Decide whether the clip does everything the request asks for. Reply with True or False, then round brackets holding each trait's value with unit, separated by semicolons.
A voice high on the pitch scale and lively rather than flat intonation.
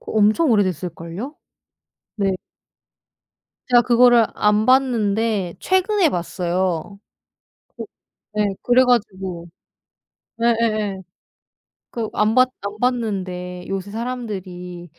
False (210 Hz; 4.4 semitones)